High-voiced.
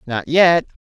No: medium, 150 Hz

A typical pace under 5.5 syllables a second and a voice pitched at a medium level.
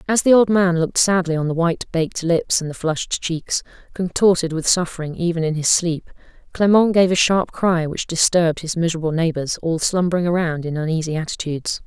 No: 5.8 syllables/s; medium, 170 Hz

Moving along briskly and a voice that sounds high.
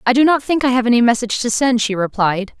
Yes: fast, 275 wpm; high, 240 Hz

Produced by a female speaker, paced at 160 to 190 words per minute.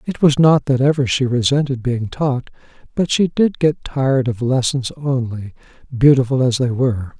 No: male; average, 175 wpm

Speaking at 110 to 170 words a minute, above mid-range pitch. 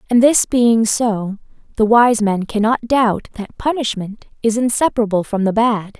Yes: average, 160 wpm; high, 225 Hz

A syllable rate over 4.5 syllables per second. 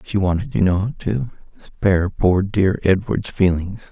No: 4.0 syllables/s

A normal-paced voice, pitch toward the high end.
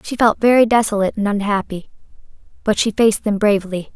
Yes: average, 165 wpm; high, 210 Hz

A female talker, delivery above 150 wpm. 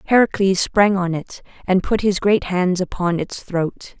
Yes: female; average, 180 wpm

